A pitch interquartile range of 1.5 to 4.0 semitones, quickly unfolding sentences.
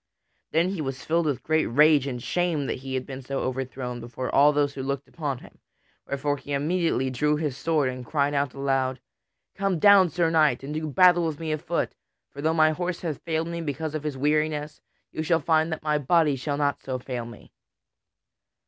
Yes: average, 3.0 semitones; fast, 210 wpm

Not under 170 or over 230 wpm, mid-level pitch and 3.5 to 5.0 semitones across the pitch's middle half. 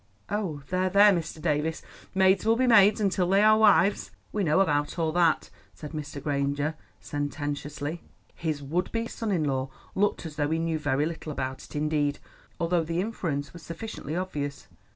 Yes: average, 175 wpm; medium, 160 Hz; average, 4.5 semitones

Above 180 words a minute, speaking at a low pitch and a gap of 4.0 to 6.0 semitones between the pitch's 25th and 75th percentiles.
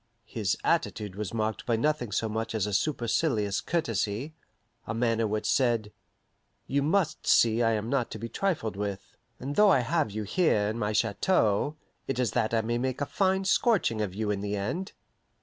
Yes: average, 190 wpm; low, 115 Hz; average, 5.0 semitones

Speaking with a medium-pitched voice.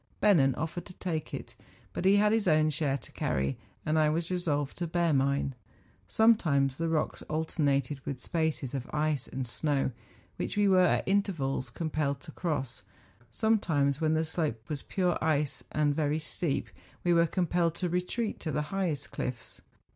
Yes: medium, 155 Hz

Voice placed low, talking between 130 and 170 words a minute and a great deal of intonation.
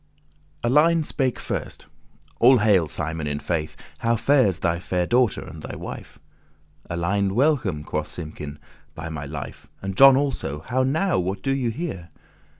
Yes: very low, 95 Hz; average, 155 wpm; wide, 8.3 semitones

